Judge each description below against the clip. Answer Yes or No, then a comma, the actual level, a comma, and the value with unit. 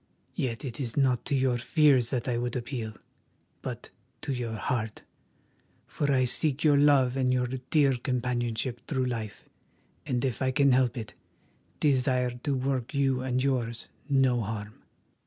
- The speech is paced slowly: No, average, 155 wpm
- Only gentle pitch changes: Yes, narrow, 2.0 semitones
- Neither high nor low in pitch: No, low, 125 Hz